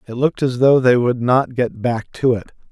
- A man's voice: Yes, male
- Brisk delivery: Yes, fast, 245 wpm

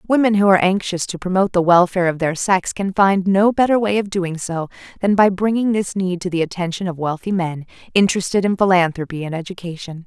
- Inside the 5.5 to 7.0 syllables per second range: Yes, 6.0 syllables/s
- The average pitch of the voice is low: No, medium, 185 Hz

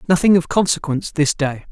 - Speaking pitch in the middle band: Yes, medium, 165 Hz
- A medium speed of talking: Yes, average, 175 wpm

